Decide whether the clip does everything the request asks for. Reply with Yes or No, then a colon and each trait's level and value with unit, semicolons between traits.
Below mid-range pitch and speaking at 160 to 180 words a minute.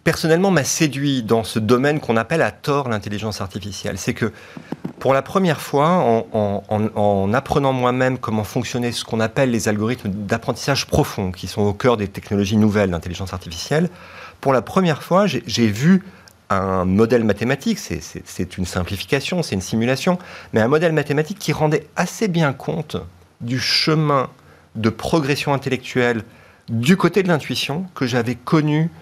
Yes: low, 125 Hz; average, 165 wpm